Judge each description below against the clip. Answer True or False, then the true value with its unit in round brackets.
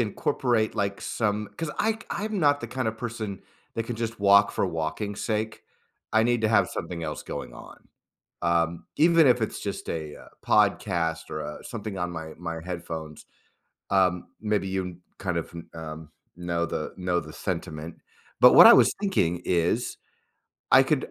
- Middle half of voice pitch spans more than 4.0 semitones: True (5.0 semitones)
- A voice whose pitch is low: True (95 Hz)